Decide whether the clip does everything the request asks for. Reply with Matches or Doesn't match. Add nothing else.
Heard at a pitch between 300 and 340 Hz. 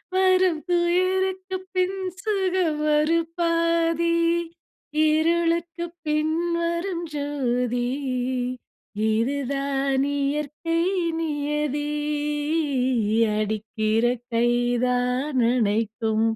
Matches